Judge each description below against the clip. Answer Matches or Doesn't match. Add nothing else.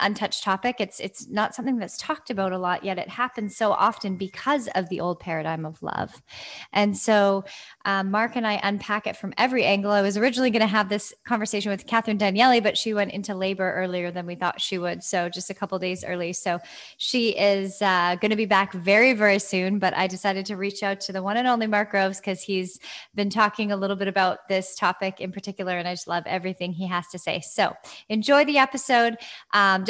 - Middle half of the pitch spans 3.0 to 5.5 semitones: Doesn't match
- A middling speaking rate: Doesn't match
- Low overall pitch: Doesn't match